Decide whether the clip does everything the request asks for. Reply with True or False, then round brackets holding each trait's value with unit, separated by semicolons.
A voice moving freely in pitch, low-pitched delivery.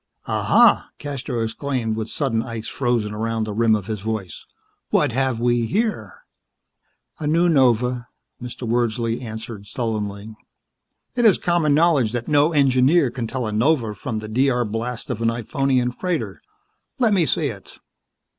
False (3.8 semitones; 120 Hz)